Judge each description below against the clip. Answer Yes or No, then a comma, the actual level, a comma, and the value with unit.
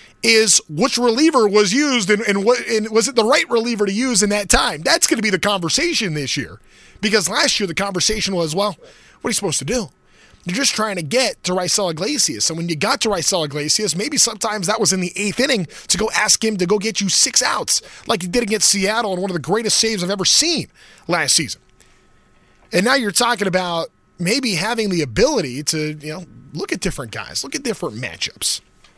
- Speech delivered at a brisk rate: Yes, fast, 225 wpm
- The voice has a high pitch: Yes, high, 210 Hz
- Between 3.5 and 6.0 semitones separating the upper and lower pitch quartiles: Yes, average, 4.2 semitones